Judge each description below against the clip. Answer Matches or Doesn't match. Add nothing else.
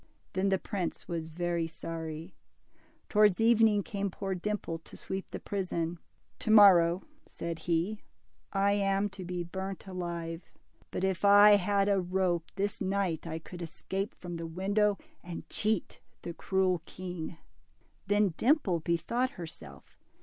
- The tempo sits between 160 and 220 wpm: Doesn't match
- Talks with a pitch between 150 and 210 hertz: Matches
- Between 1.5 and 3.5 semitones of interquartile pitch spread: Matches